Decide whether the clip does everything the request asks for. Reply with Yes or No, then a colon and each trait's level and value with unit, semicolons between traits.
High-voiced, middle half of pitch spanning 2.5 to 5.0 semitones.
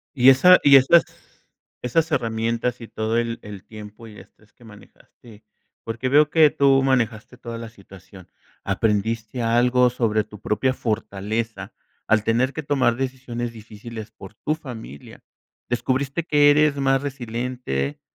No: low, 120 Hz; average, 3.4 semitones